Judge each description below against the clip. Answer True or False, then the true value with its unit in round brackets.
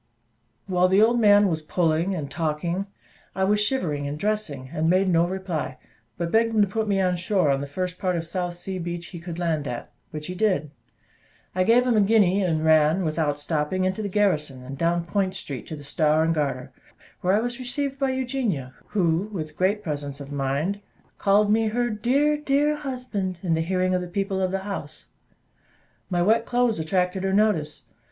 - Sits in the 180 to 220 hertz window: True (185 Hz)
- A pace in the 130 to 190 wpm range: False (200 wpm)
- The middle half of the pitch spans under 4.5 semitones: False (4.8 semitones)